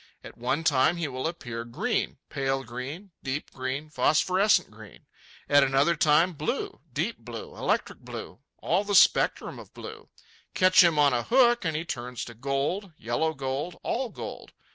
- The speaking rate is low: No, average, 155 wpm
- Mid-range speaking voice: Yes, medium, 145 Hz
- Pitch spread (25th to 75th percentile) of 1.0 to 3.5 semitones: No, average, 5.0 semitones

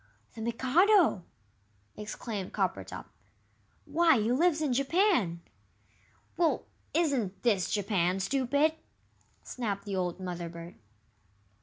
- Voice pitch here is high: Yes, high, 230 Hz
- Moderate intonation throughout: No, wide, 8.2 semitones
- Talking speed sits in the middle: No, slow, 100 wpm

